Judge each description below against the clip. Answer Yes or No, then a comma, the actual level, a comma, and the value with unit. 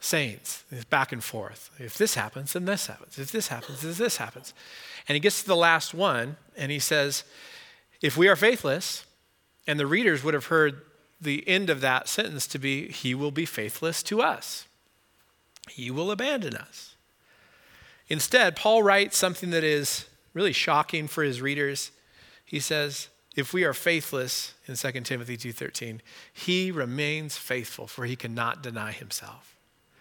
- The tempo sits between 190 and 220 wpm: No, average, 165 wpm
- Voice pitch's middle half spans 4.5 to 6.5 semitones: Yes, average, 5.0 semitones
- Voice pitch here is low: No, medium, 150 Hz